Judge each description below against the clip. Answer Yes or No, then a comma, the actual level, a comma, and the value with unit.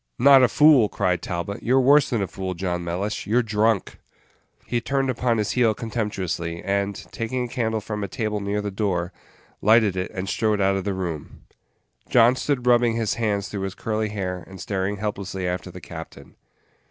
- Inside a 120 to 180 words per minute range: No, average, 190 wpm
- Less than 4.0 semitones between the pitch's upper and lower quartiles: Yes, average, 3.4 semitones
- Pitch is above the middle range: No, low, 105 Hz